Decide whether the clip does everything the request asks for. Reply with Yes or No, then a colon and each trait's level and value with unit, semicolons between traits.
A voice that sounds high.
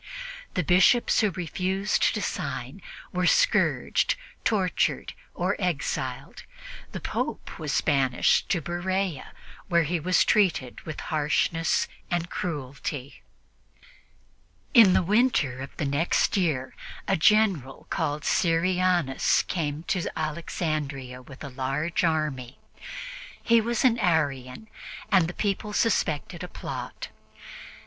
No: medium, 170 Hz